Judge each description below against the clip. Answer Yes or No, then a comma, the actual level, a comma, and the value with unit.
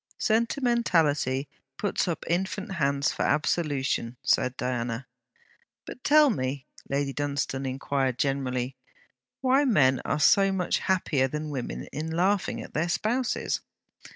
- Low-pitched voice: No, medium, 145 Hz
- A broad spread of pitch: Yes, wide, 6.5 semitones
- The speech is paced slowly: Yes, slow, 125 wpm